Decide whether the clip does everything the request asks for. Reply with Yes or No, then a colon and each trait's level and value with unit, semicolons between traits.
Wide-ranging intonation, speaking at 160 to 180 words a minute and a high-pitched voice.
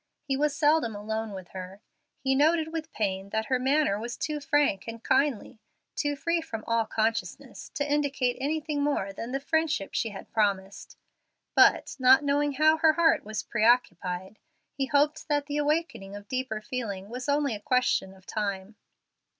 Yes: wide, 5.7 semitones; average, 170 wpm; very high, 255 Hz